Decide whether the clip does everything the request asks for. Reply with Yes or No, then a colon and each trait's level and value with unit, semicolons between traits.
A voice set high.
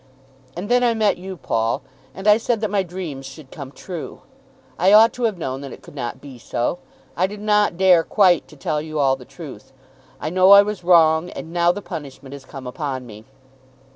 No: medium, 170 Hz